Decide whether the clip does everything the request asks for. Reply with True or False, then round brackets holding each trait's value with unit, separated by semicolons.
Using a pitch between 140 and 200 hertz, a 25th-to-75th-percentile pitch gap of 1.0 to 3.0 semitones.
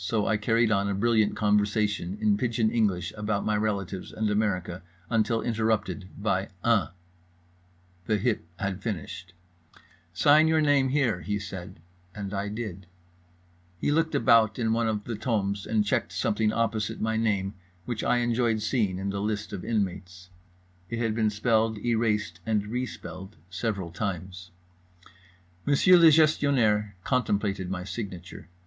False (105 Hz; 2.6 semitones)